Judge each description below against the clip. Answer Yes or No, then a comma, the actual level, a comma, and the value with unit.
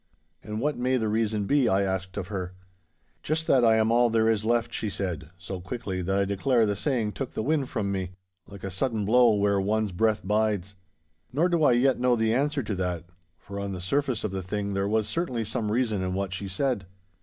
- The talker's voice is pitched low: Yes, low, 110 Hz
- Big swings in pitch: No, average, 3.8 semitones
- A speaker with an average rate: No, fast, 225 wpm